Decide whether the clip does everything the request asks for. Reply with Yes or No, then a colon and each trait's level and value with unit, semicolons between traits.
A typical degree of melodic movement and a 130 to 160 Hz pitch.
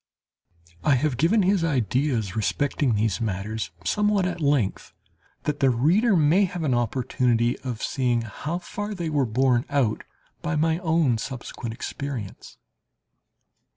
No: wide, 5.8 semitones; low, 135 Hz